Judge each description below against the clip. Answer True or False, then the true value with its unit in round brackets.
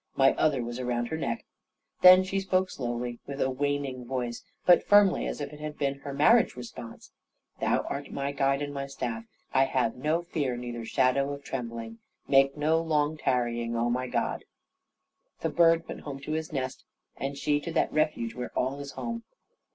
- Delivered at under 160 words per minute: False (190 wpm)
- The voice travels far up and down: False (3.7 semitones)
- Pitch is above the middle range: False (140 Hz)